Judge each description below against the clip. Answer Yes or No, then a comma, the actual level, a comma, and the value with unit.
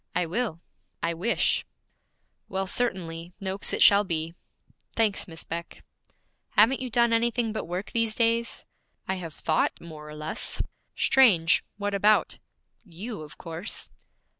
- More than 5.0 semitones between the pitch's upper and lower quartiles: Yes, wide, 5.5 semitones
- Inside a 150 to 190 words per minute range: No, average, 140 wpm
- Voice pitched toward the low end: No, high, 190 Hz